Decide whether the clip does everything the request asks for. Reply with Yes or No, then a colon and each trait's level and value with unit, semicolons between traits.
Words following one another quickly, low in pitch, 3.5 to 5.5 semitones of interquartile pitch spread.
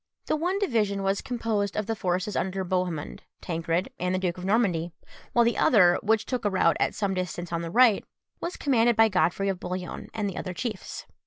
No: fast, 210 wpm; high, 195 Hz; average, 3.8 semitones